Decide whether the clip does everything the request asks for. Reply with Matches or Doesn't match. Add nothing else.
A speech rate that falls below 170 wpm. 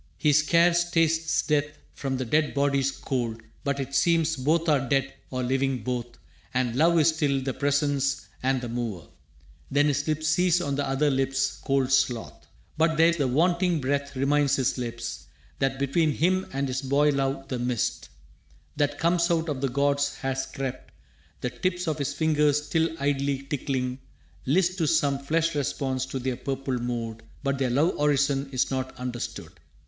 Doesn't match